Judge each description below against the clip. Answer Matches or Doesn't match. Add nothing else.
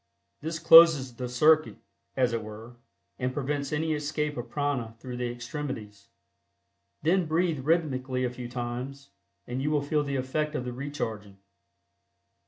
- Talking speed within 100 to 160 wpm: Matches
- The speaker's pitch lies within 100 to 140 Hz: Matches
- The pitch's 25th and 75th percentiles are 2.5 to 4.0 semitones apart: Matches